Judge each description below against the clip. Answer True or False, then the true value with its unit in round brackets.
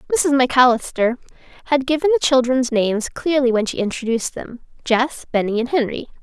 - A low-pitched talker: False (255 Hz)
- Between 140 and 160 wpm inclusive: True (145 wpm)